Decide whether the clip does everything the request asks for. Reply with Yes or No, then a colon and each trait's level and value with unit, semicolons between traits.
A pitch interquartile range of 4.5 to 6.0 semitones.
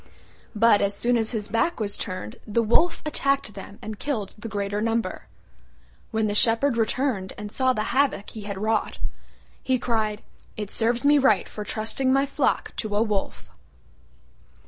No: average, 3.2 semitones